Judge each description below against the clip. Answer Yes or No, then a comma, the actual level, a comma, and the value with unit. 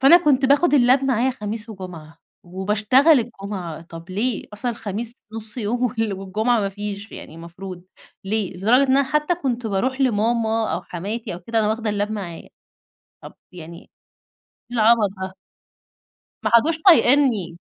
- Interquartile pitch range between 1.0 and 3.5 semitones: No, average, 4.3 semitones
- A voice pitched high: Yes, high, 220 Hz